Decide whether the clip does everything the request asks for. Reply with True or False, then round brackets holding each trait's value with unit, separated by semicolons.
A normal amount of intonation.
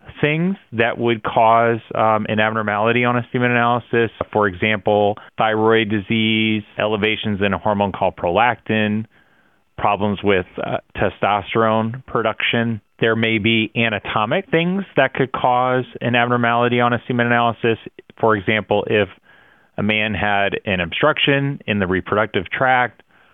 False (2.2 semitones)